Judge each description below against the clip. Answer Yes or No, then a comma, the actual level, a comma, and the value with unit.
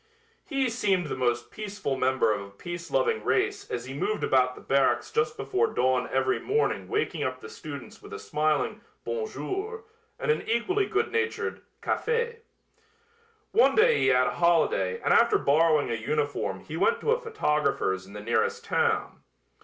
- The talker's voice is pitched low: No, medium, 170 Hz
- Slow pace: No, average, 175 wpm